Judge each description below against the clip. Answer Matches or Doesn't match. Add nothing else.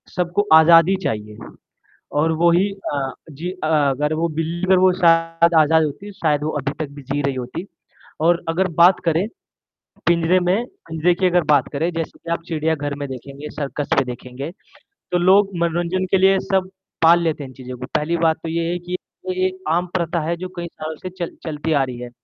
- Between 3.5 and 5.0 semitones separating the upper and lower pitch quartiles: Doesn't match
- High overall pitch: Doesn't match